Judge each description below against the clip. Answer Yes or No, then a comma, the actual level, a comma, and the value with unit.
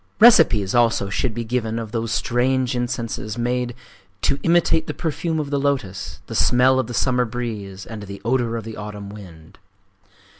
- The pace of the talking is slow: No, average, 175 wpm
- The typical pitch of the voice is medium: No, low, 120 Hz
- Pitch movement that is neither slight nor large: Yes, average, 3.4 semitones